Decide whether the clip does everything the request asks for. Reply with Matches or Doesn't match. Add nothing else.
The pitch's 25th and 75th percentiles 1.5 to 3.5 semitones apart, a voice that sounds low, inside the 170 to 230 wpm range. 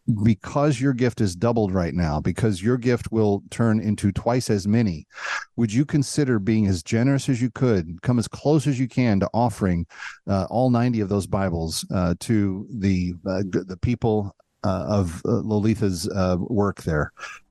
Doesn't match